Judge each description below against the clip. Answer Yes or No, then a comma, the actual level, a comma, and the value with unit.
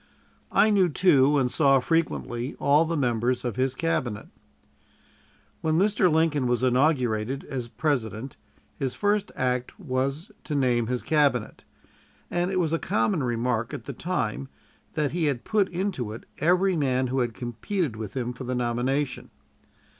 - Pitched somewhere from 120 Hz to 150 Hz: Yes, low, 135 Hz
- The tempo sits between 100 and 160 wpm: Yes, average, 155 wpm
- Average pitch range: Yes, average, 4.8 semitones